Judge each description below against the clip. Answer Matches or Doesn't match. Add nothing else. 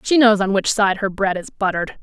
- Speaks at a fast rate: Matches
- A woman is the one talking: Matches